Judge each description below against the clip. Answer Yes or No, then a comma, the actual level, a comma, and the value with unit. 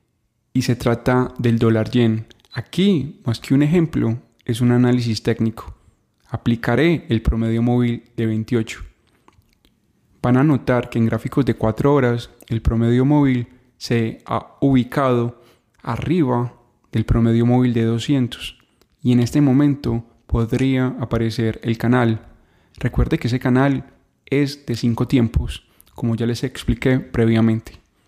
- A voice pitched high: No, low, 120 Hz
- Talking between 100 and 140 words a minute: Yes, average, 135 wpm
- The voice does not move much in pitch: Yes, narrow, 1.9 semitones